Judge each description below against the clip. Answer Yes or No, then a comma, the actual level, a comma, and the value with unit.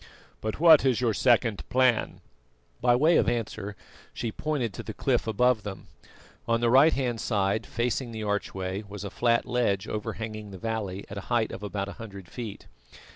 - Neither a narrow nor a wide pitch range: Yes, average, 3.1 semitones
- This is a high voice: No, low, 110 Hz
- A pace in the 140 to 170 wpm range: No, average, 180 wpm